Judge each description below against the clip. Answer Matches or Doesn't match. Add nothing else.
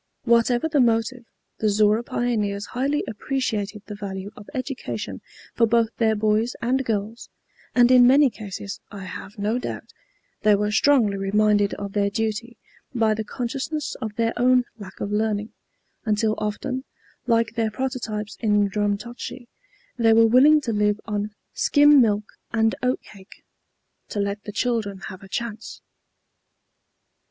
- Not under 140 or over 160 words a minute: Matches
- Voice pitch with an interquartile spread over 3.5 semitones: Doesn't match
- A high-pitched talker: Matches